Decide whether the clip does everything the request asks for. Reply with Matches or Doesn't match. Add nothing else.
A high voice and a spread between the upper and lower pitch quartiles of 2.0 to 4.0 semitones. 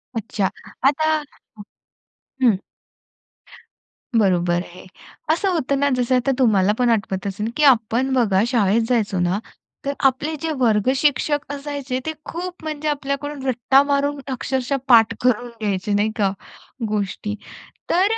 Doesn't match